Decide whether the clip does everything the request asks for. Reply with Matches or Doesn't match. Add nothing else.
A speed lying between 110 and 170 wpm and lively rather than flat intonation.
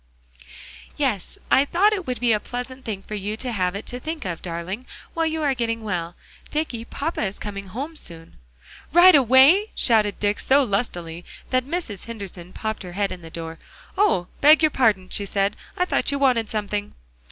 Doesn't match